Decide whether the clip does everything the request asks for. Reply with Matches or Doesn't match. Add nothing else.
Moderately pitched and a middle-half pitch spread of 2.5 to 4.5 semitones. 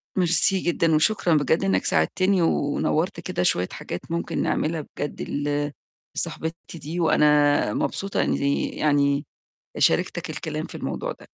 Matches